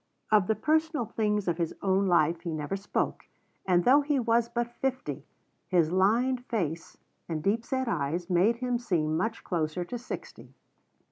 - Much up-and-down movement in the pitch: Yes, wide, 5.7 semitones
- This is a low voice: No, high, 205 Hz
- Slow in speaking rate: No, average, 165 wpm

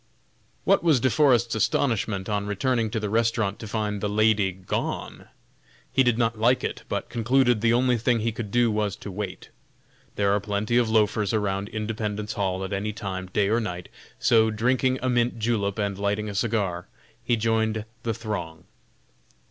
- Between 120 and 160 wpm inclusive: No, average, 180 wpm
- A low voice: Yes, low, 110 Hz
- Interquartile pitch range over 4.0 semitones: No, narrow, 2.5 semitones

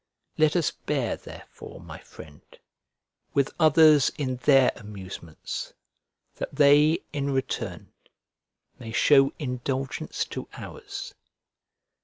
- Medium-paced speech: No, slow, 100 wpm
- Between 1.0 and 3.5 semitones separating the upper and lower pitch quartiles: Yes, average, 2.9 semitones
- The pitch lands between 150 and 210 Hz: No, low, 135 Hz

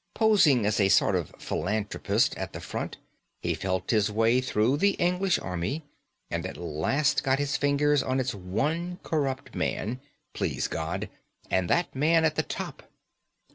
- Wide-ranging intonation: Yes, wide, 7.1 semitones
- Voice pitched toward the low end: Yes, low, 130 Hz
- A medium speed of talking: Yes, average, 160 wpm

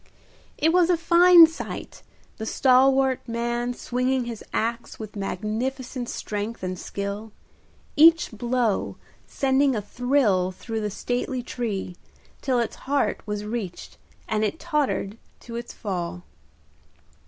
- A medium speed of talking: No, slow, 125 wpm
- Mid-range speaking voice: No, high, 240 Hz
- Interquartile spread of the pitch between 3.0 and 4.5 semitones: Yes, average, 4.0 semitones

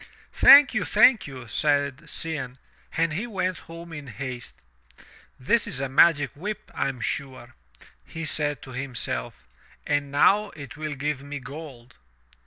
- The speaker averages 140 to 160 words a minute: Yes, average, 155 wpm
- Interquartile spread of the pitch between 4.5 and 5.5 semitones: No, average, 3.8 semitones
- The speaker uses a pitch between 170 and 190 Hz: No, medium, 145 Hz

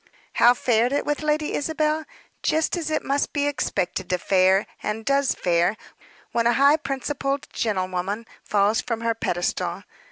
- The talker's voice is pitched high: Yes, high, 245 Hz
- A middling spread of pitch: No, wide, 6.1 semitones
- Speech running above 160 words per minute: No, average, 155 wpm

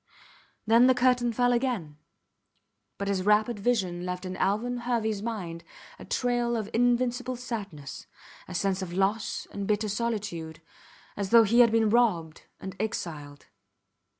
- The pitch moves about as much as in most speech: Yes, average, 4.4 semitones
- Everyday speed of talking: Yes, average, 145 wpm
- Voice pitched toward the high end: Yes, high, 215 Hz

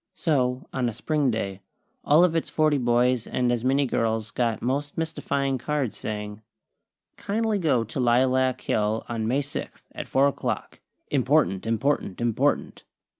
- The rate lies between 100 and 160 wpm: Yes, average, 150 wpm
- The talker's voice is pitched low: Yes, low, 125 Hz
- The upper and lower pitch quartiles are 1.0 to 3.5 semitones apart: No, average, 4.0 semitones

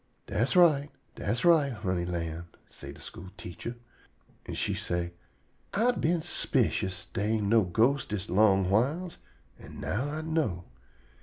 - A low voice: Yes, low, 110 Hz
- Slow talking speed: No, average, 145 wpm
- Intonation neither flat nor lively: No, wide, 8.1 semitones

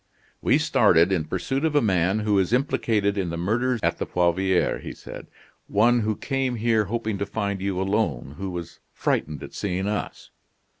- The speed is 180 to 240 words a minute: Yes, average, 185 wpm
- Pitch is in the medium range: No, low, 100 Hz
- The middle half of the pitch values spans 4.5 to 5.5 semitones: No, average, 3.6 semitones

